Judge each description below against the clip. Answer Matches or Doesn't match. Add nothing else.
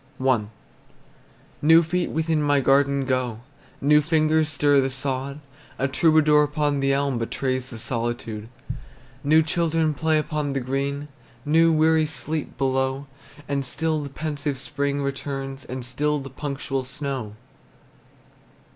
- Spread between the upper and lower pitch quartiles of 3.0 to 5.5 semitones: Doesn't match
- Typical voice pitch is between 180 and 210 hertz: Doesn't match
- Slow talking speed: Matches